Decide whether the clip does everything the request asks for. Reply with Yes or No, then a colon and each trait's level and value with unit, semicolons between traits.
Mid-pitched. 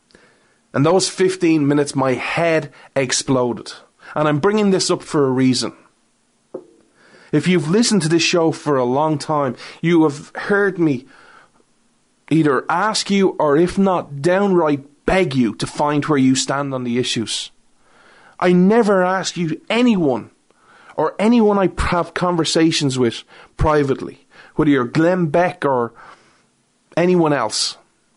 Yes: medium, 160 Hz